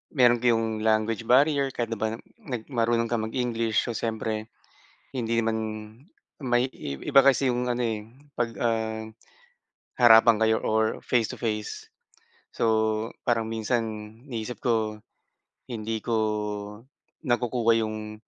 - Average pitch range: No, narrow, 1.7 semitones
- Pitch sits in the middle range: No, low, 115 Hz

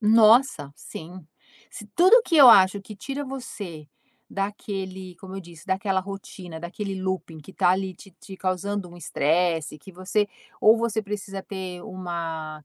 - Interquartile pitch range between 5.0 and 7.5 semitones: No, average, 2.9 semitones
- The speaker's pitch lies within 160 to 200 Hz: Yes, high, 190 Hz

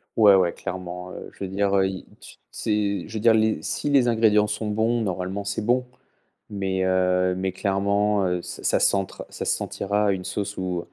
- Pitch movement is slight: Yes, narrow, 2.2 semitones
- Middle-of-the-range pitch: No, low, 100 Hz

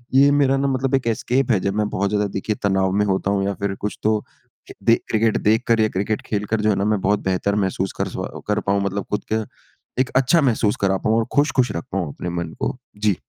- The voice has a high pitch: No, low, 105 Hz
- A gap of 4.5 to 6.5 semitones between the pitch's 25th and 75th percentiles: No, average, 2.7 semitones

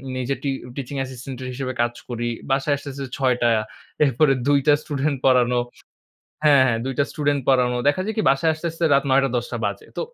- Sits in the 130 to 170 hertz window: Yes, low, 135 Hz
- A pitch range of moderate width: No, narrow, 2.3 semitones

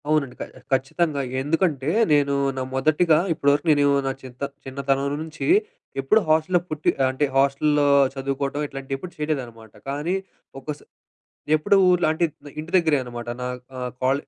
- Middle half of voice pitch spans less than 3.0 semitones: Yes, narrow, 2.6 semitones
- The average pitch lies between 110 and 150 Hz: Yes, medium, 140 Hz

